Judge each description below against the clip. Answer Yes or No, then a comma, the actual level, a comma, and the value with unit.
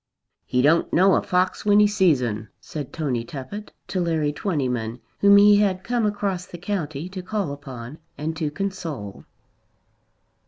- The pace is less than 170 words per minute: Yes, average, 160 wpm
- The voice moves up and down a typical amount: No, wide, 6.0 semitones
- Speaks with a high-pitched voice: No, medium, 170 Hz